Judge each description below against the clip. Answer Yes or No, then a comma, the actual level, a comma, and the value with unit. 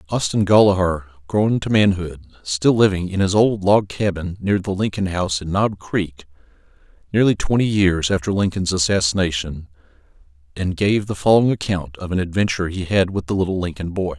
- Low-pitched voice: Yes, very low, 90 Hz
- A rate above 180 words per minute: No, average, 170 wpm